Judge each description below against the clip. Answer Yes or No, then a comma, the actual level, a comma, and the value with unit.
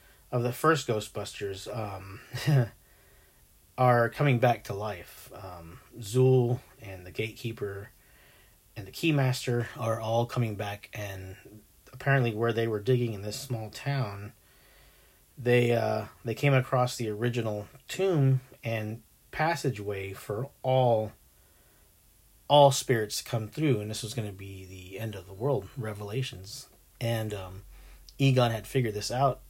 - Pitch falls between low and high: No, low, 115 Hz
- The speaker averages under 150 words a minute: Yes, average, 140 wpm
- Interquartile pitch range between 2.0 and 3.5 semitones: No, average, 3.9 semitones